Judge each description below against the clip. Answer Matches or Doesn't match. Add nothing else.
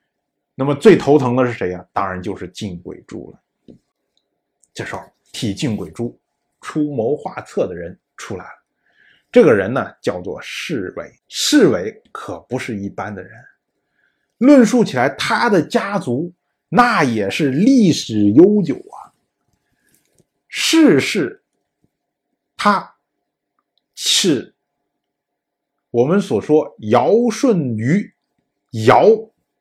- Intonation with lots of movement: Matches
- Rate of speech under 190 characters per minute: Matches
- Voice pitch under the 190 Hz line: Matches